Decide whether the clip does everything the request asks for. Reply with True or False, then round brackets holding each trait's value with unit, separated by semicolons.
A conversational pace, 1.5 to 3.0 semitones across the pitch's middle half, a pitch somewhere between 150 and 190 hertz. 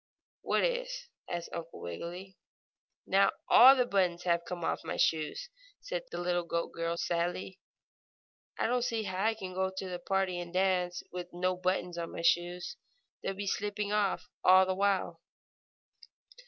True (170 wpm; 2.6 semitones; 185 Hz)